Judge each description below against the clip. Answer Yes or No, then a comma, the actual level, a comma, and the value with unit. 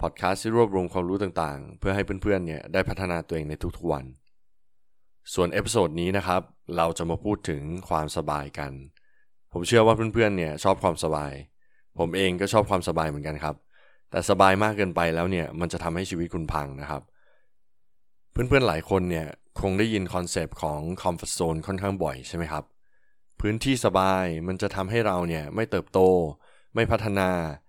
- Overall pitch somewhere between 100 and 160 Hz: No, very low, 90 Hz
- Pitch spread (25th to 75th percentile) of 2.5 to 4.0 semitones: Yes, average, 3.3 semitones